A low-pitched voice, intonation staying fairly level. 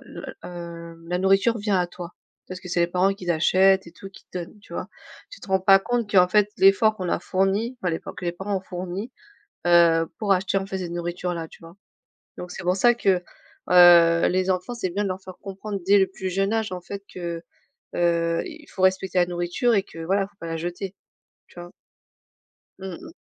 No: medium, 185 Hz; narrow, 2.0 semitones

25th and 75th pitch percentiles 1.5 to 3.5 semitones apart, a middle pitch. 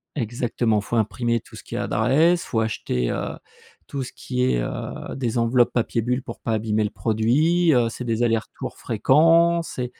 No: average, 2.9 semitones; low, 120 Hz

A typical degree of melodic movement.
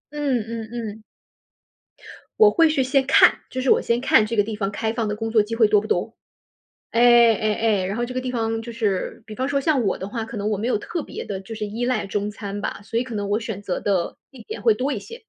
Yes: average, 3.0 semitones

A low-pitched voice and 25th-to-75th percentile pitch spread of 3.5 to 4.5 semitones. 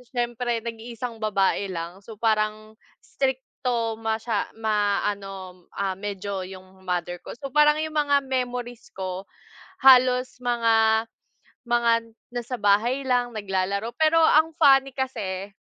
No: high, 225 Hz; average, 3.9 semitones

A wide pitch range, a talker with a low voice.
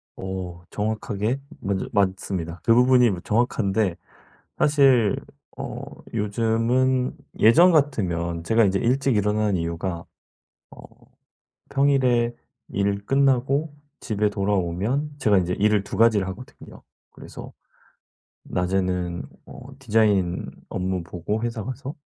No: average, 4.8 semitones; low, 105 Hz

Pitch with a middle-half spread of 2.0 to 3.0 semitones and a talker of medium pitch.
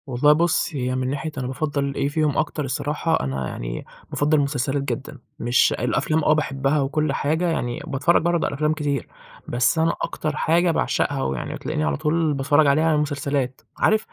Yes: narrow, 2.6 semitones; medium, 145 Hz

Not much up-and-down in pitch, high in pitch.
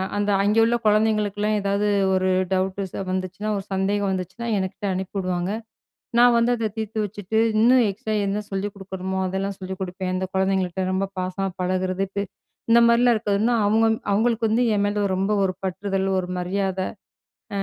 Yes: narrow, 2.2 semitones; high, 195 Hz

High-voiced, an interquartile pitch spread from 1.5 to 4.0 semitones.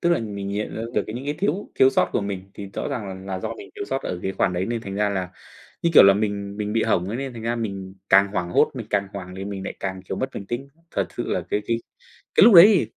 No: low, 100 Hz; average, 3.7 semitones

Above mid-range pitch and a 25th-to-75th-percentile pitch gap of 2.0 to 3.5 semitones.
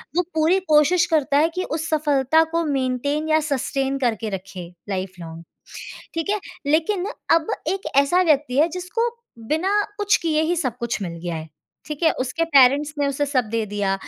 No: very high, 290 Hz; average, 4.8 semitones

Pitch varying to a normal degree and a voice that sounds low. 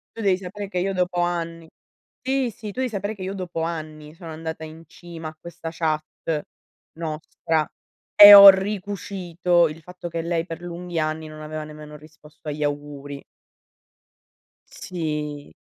No: average, 3.0 semitones; medium, 165 Hz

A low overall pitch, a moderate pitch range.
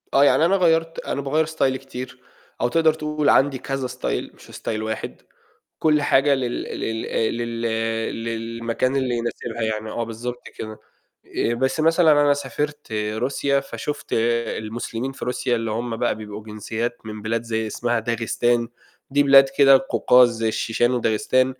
Yes: low, 120 Hz; average, 3.4 semitones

